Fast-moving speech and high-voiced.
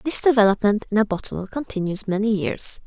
No: average, 165 wpm; high, 215 Hz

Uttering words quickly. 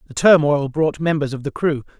Yes: fast, 210 wpm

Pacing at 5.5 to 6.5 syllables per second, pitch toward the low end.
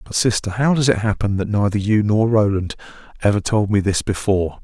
Yes: 5.7 syllables/s; low, 105 Hz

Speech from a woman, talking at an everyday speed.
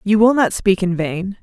No: female; fast, 255 wpm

